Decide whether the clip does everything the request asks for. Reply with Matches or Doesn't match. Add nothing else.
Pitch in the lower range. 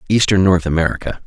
Matches